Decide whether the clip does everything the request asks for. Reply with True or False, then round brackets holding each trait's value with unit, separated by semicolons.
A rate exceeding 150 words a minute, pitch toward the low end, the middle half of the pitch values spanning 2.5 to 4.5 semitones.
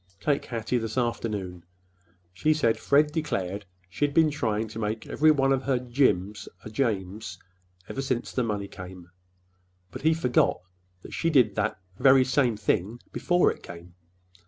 False (160 wpm; 120 Hz; 5.1 semitones)